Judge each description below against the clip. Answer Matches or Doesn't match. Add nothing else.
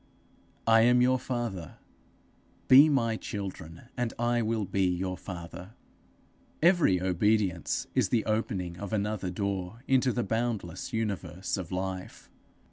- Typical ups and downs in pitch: Matches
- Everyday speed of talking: Doesn't match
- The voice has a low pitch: Matches